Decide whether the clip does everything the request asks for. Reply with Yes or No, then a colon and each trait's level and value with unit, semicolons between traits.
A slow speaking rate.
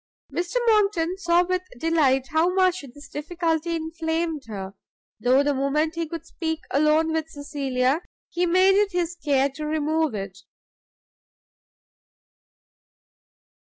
Yes: slow, 120 wpm